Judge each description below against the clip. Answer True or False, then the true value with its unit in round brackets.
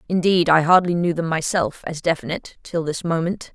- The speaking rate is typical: True (185 wpm)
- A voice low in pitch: False (170 Hz)